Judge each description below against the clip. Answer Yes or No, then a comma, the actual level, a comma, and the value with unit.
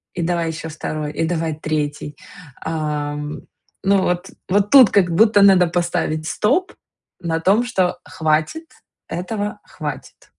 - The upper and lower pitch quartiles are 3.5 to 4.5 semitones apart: Yes, average, 4.1 semitones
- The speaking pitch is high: No, medium, 175 Hz